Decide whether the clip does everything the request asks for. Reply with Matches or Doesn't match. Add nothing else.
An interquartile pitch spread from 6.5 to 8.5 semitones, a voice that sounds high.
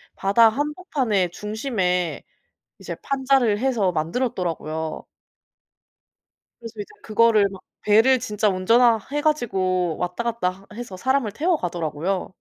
Doesn't match